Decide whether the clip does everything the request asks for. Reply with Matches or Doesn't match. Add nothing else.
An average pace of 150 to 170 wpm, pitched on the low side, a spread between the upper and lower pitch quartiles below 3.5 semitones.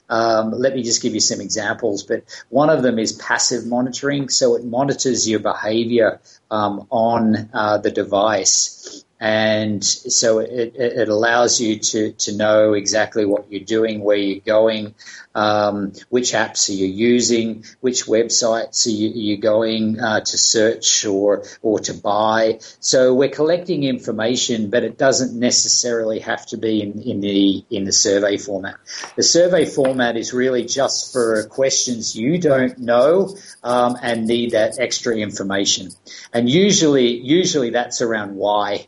Matches